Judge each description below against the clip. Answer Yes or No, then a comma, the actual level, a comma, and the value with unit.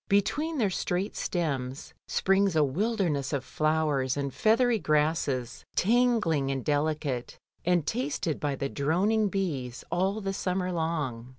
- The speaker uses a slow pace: Yes, slow, 130 wpm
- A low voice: No, medium, 165 Hz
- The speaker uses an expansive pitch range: Yes, wide, 6.0 semitones